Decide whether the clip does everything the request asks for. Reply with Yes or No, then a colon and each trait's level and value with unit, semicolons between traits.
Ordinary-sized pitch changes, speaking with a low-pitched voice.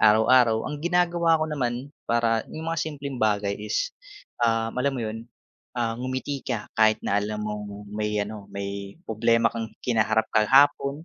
Yes: average, 4.5 semitones; low, 115 Hz